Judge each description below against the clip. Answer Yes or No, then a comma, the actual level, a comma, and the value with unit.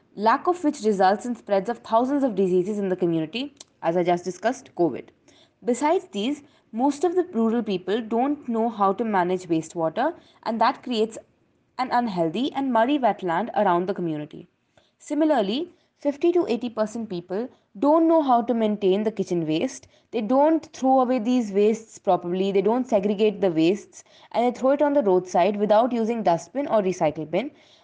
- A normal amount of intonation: No, wide, 5.7 semitones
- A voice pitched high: Yes, high, 225 Hz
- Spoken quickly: No, average, 175 wpm